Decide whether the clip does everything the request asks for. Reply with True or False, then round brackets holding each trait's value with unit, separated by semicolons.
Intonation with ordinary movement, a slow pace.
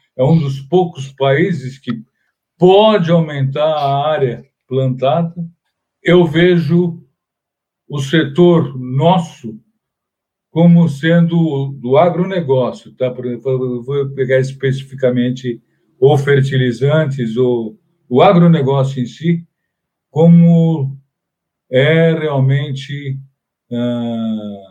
True (4.3 semitones; 90 wpm)